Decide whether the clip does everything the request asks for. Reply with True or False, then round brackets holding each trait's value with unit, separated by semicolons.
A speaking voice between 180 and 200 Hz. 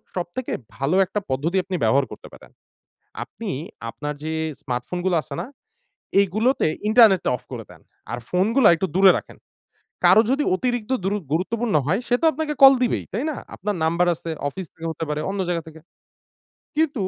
True (190 Hz)